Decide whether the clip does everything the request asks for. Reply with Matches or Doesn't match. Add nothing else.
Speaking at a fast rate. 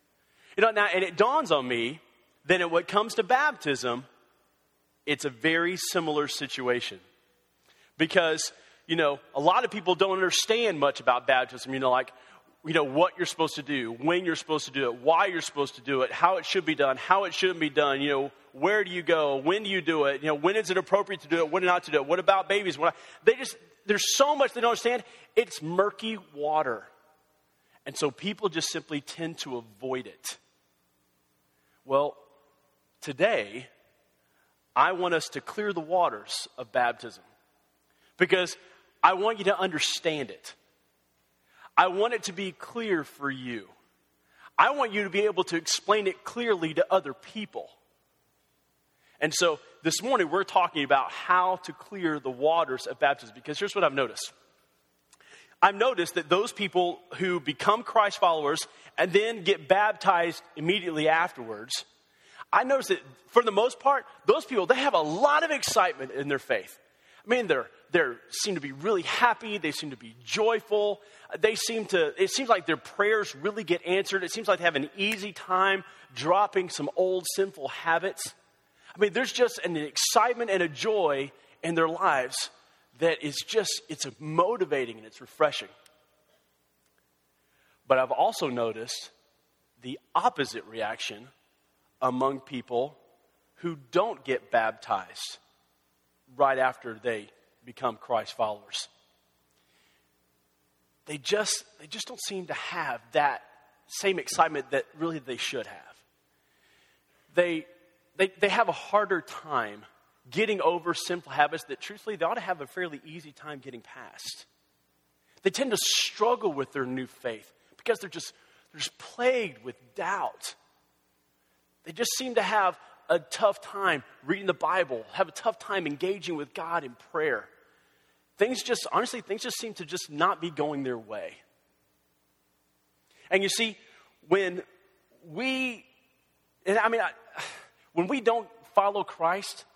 Doesn't match